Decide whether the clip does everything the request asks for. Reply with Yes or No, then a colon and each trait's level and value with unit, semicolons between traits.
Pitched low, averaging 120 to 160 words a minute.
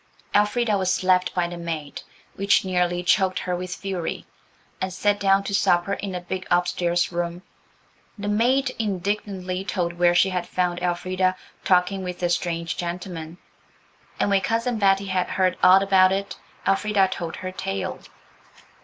No: medium, 185 Hz; average, 155 wpm